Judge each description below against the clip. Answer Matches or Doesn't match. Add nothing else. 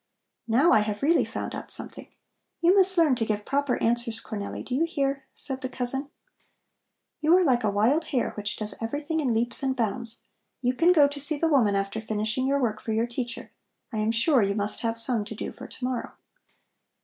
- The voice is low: Doesn't match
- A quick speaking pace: Matches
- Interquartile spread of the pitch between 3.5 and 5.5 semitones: Matches